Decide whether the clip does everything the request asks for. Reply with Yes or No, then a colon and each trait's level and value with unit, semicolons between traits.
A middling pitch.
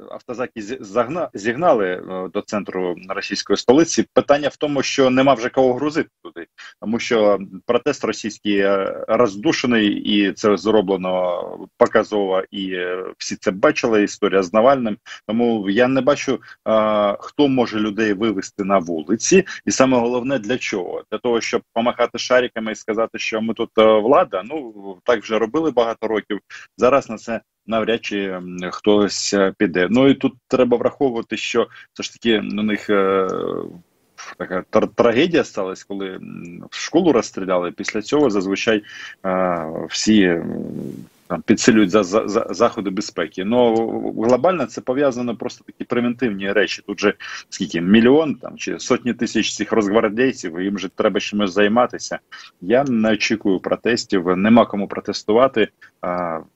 No: low, 110 Hz